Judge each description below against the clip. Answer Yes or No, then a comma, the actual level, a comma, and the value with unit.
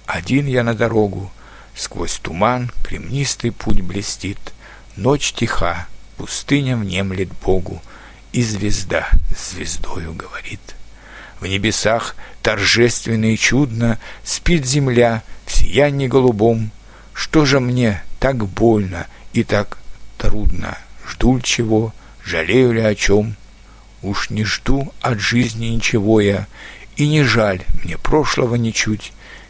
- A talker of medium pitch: No, low, 110 Hz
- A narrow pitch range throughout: No, average, 3.4 semitones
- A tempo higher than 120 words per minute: No, average, 115 wpm